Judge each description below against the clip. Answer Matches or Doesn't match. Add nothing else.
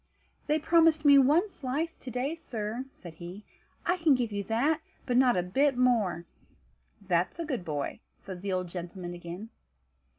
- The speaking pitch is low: Doesn't match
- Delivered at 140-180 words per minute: Matches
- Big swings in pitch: Matches